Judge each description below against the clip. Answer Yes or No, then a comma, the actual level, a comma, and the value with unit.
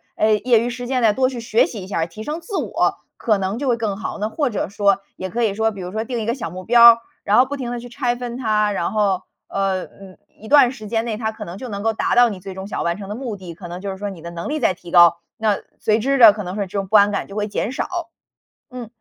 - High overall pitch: Yes, high, 215 Hz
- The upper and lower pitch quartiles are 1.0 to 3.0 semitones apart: No, average, 3.7 semitones